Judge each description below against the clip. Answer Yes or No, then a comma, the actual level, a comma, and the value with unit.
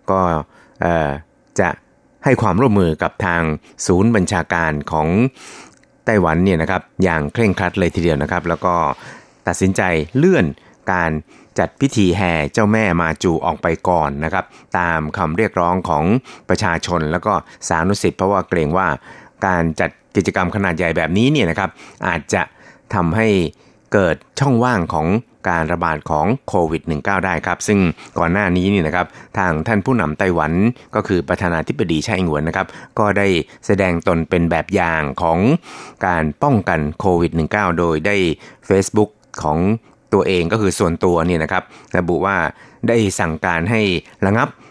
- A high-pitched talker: No, very low, 90 Hz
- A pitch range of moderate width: Yes, average, 3.4 semitones